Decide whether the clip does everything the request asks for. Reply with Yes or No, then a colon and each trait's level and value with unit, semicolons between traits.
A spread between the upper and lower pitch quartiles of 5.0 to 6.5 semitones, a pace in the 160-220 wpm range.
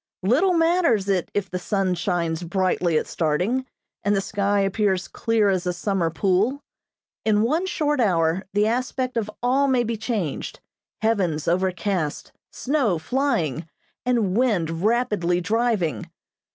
No: average, 5.3 semitones; average, 140 wpm